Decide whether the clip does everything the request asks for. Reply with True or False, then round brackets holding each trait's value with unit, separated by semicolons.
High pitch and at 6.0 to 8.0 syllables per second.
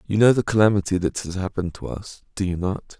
False (95 Hz; 6.1 syllables/s)